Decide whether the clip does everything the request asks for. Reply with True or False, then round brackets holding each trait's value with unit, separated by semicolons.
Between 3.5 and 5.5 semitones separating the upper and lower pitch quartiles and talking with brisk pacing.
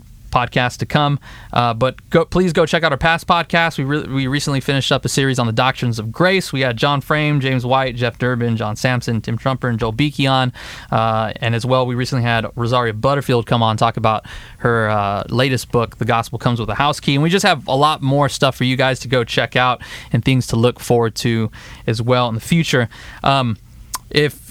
False (3.1 semitones; 235 wpm)